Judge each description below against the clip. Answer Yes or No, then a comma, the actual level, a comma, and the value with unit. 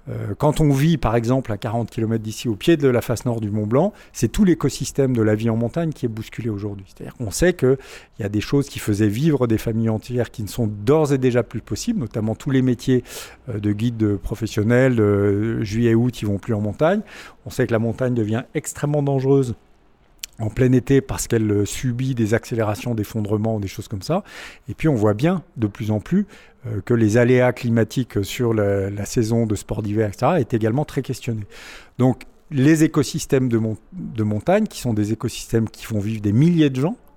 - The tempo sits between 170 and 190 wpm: No, average, 210 wpm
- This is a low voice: Yes, low, 115 Hz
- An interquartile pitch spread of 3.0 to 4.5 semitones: Yes, average, 3.9 semitones